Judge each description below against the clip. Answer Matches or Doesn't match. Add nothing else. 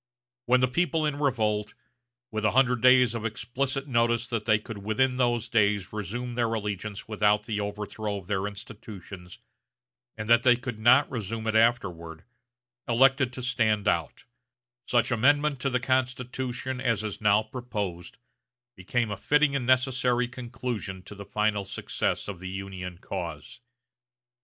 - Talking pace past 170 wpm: Doesn't match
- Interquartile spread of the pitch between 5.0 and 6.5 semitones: Doesn't match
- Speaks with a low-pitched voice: Matches